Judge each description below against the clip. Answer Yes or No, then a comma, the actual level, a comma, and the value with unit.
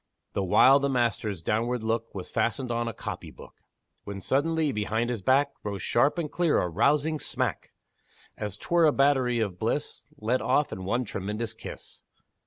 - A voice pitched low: Yes, low, 120 Hz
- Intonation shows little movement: No, average, 4.9 semitones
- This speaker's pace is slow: No, average, 175 wpm